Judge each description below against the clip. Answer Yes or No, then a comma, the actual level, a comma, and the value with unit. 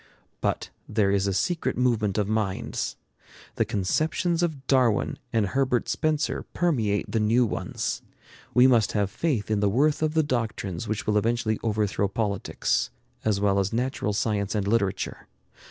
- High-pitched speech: No, low, 110 Hz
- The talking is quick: No, average, 155 wpm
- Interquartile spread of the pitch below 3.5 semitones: No, average, 4.1 semitones